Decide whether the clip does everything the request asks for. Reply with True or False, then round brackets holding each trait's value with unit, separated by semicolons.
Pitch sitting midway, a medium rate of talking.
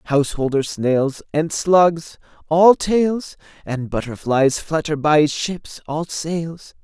False (155 Hz; 105 wpm)